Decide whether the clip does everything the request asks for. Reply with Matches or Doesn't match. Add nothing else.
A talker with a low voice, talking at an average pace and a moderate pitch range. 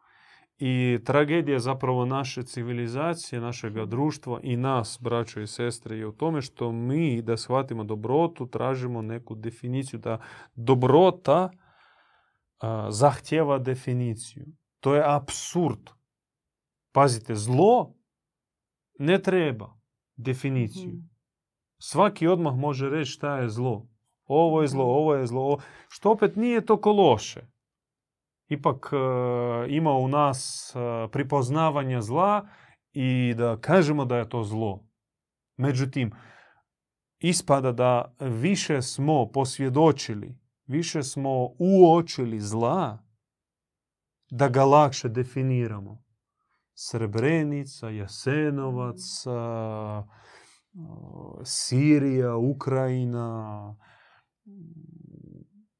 Doesn't match